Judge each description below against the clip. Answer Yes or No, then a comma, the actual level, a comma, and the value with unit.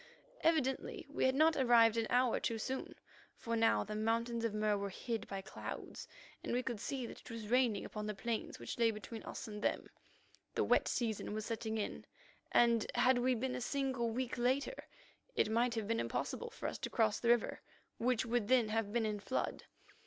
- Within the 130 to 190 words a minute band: No, fast, 205 wpm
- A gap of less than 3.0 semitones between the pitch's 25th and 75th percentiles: Yes, narrow, 2.6 semitones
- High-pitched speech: Yes, high, 230 Hz